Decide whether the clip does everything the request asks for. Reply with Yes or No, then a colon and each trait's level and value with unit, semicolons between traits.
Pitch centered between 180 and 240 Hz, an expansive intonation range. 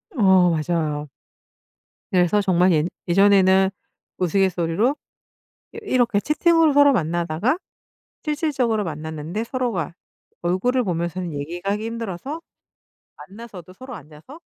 Yes: high, 190 Hz; wide, 5.8 semitones